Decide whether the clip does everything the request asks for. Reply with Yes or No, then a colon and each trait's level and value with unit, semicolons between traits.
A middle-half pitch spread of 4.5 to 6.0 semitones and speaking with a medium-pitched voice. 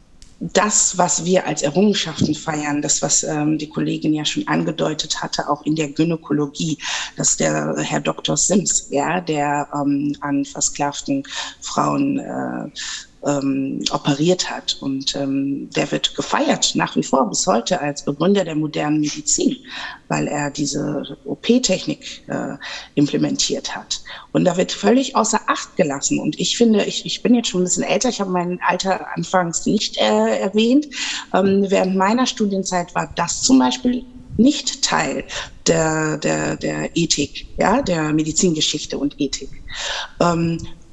Yes: average, 5.0 semitones; medium, 155 Hz